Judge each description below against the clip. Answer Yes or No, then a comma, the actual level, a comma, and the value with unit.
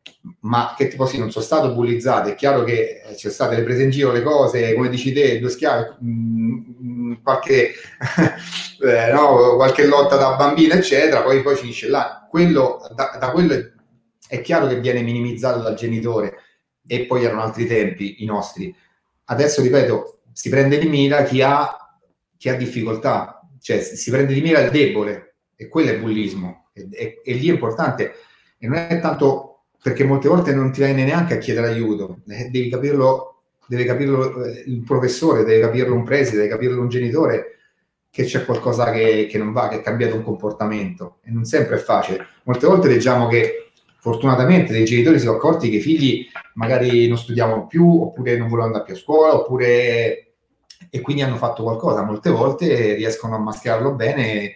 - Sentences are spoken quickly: Yes, fast, 185 wpm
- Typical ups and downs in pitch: Yes, average, 4.1 semitones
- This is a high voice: No, low, 125 Hz